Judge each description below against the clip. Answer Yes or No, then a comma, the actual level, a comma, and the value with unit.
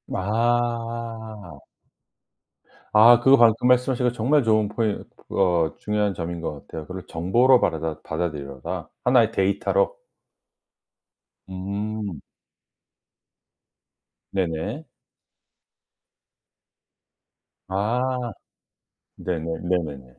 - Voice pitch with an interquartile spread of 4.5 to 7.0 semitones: Yes, wide, 5.5 semitones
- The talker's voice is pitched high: No, low, 105 Hz